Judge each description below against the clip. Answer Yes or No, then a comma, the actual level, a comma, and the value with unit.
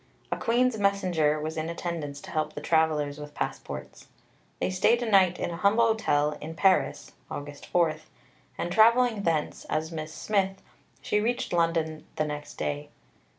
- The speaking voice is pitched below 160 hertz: No, medium, 170 Hz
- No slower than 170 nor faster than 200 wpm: No, average, 155 wpm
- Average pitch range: Yes, average, 4.5 semitones